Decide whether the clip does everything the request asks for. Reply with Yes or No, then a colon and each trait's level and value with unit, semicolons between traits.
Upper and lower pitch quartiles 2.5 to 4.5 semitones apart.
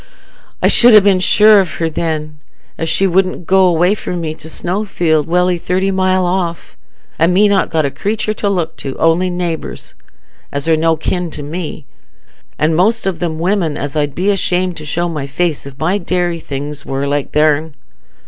Yes: average, 3.2 semitones